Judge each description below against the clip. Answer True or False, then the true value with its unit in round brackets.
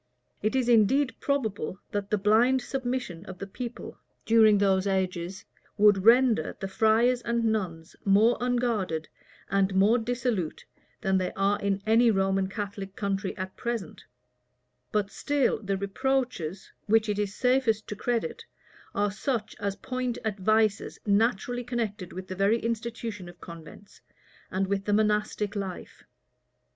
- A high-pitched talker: True (210 Hz)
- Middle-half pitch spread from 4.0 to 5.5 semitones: False (3.4 semitones)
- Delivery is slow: False (145 wpm)